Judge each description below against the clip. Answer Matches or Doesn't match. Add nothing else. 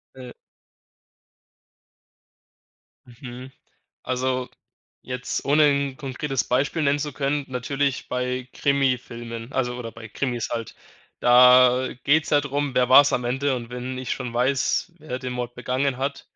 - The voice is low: Matches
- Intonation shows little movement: Matches